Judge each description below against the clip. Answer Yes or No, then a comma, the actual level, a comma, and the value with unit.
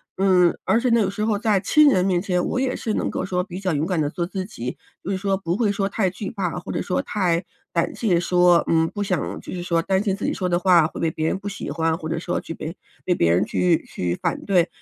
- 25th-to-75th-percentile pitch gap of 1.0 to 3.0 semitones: Yes, average, 2.7 semitones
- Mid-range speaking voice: Yes, medium, 180 Hz